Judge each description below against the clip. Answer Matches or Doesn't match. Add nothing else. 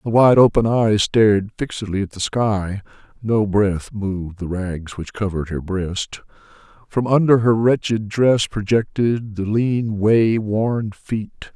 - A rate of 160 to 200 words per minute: Doesn't match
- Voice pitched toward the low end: Matches